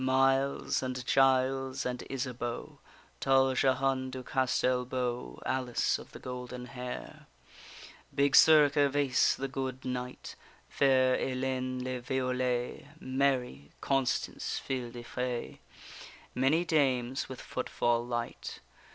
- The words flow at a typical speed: No, slow, 110 wpm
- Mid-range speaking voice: No, low, 130 Hz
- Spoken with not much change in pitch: Yes, narrow, 1.2 semitones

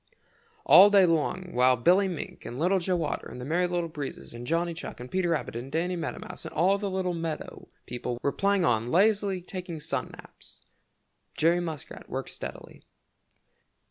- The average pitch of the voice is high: No, medium, 170 Hz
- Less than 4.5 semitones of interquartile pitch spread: Yes, average, 3.7 semitones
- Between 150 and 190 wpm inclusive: Yes, average, 185 wpm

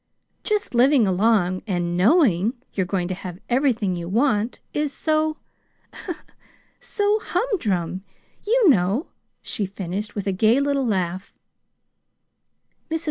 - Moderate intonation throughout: No, wide, 7.4 semitones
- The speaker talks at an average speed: No, slow, 115 wpm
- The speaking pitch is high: Yes, high, 210 Hz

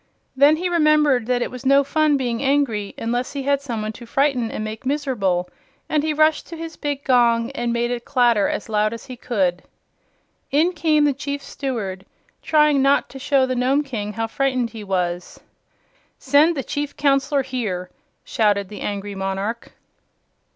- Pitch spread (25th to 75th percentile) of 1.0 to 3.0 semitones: No, average, 4.5 semitones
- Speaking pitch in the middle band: No, very high, 255 Hz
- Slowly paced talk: No, average, 180 wpm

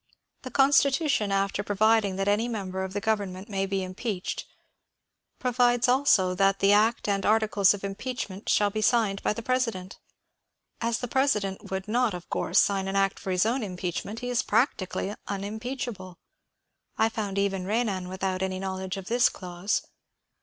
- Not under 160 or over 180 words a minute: Yes, average, 170 wpm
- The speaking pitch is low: No, high, 205 Hz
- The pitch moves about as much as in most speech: Yes, average, 3.2 semitones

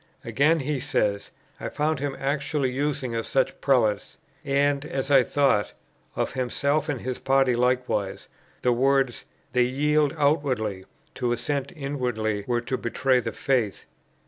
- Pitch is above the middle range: No, low, 135 Hz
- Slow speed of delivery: No, average, 145 wpm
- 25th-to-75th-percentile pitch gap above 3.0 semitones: No, average, 2.7 semitones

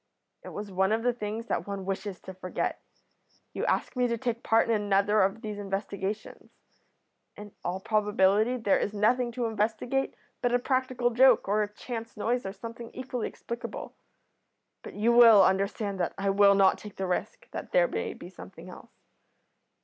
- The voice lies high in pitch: Yes, high, 215 Hz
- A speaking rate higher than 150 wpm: Yes, average, 180 wpm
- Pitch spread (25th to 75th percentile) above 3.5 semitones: No, average, 3.1 semitones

